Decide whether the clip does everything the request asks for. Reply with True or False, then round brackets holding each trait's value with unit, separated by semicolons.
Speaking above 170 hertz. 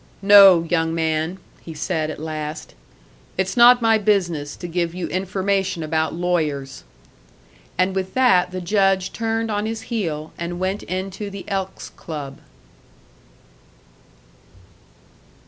True (185 Hz)